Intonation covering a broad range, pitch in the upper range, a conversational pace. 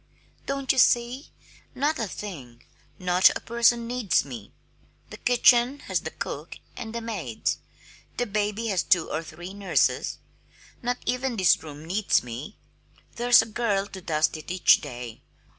Yes: wide, 6.7 semitones; high, 205 Hz; average, 155 wpm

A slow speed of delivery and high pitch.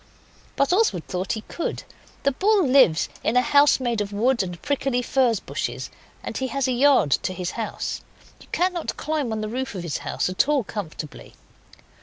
No: average, 190 wpm; very high, 250 Hz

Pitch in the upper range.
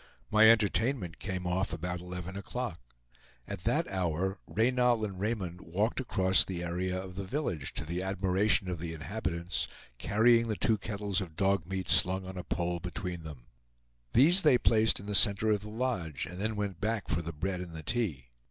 No: very low, 95 Hz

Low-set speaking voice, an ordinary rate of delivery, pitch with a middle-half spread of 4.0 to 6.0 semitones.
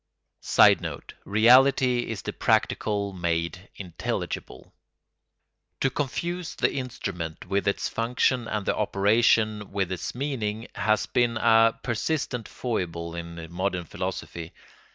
No: low, 105 Hz; slow, 110 wpm; average, 5.1 semitones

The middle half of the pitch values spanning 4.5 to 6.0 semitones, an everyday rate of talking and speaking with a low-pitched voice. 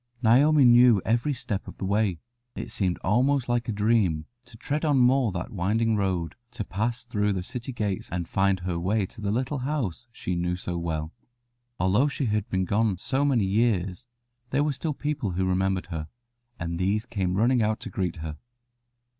Yes: average, 4.8 semitones; average, 190 wpm; low, 105 Hz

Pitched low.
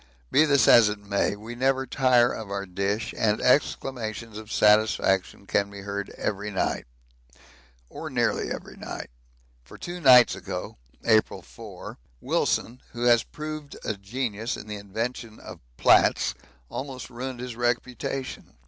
Yes: low, 115 Hz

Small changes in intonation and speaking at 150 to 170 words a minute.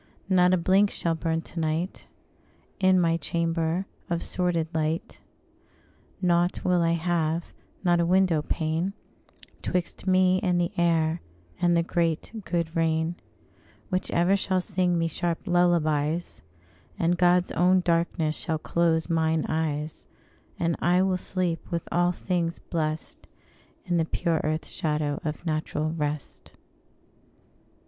No: narrow, 1.8 semitones; slow, 135 wpm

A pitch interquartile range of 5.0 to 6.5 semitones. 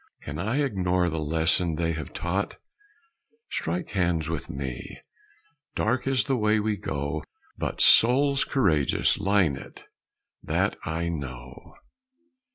Yes: wide, 5.4 semitones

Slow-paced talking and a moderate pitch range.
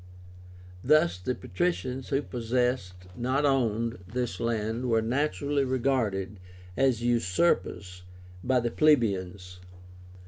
Yes: slow, 100 wpm; average, 4.4 semitones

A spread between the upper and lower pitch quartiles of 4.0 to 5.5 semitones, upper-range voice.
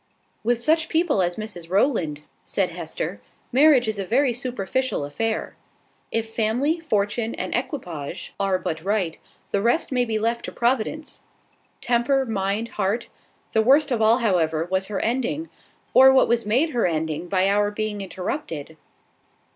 Yes: average, 5.0 semitones; high, 220 Hz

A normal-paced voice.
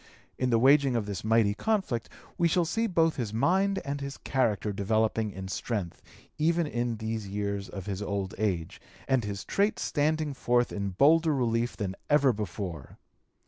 Yes: average, 170 wpm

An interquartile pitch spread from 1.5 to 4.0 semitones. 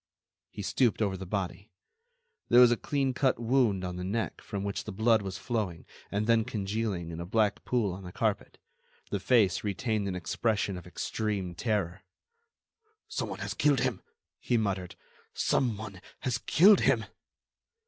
Yes: average, 3.5 semitones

